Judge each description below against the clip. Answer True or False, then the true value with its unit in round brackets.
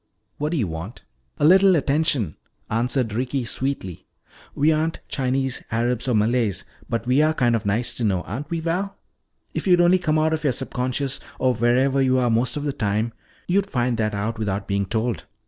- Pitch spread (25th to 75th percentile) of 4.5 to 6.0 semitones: True (4.8 semitones)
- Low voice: True (125 Hz)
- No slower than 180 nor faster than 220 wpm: True (195 wpm)